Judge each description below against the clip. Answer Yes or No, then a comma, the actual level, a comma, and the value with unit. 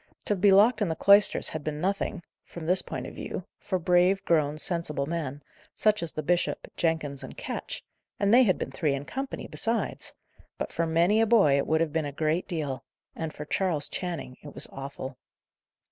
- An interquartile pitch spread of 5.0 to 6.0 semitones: No, average, 4.4 semitones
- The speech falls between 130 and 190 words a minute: No, average, 200 wpm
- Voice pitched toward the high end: No, medium, 165 Hz